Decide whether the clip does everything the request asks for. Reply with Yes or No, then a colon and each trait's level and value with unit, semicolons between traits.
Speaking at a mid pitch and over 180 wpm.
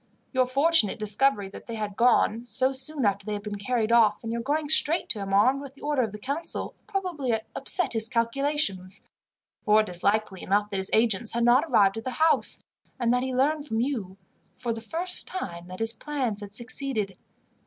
No: high, 230 Hz; fast, 205 wpm